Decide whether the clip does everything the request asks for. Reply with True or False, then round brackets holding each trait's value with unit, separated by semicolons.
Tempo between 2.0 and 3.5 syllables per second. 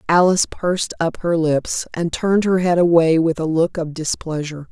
False (5.2 syllables/s)